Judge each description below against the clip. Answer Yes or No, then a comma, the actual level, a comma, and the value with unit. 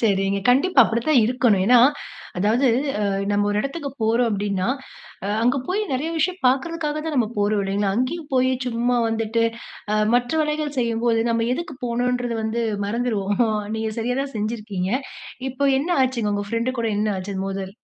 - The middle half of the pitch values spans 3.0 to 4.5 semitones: Yes, average, 3.8 semitones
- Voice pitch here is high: Yes, high, 235 Hz